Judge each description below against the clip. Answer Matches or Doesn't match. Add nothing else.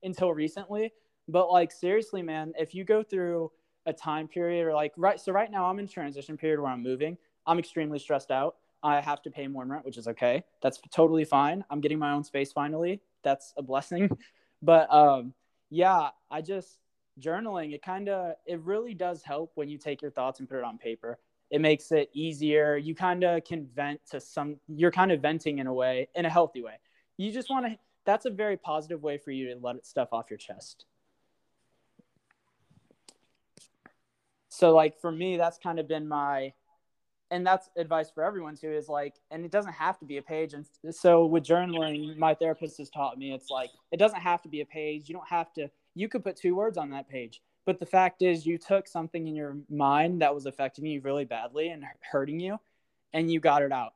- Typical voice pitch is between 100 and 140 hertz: Doesn't match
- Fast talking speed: Matches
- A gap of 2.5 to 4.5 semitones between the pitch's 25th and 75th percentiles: Matches